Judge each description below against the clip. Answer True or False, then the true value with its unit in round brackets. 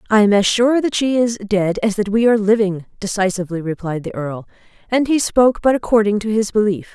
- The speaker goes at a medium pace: False (215 wpm)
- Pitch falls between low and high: False (210 Hz)